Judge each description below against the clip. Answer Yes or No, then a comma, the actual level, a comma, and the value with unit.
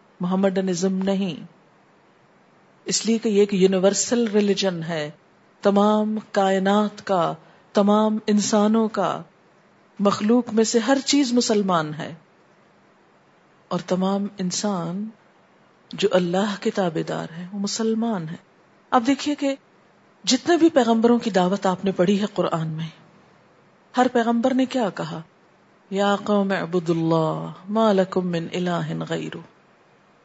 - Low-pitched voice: No, high, 200 Hz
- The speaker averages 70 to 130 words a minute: Yes, average, 125 wpm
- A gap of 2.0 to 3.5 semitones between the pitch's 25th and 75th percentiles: Yes, average, 3.2 semitones